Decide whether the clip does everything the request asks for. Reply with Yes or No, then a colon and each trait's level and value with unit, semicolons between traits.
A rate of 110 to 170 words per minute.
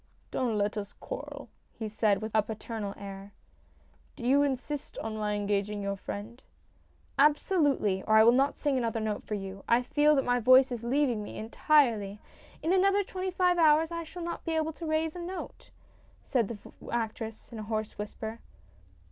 No: average, 190 wpm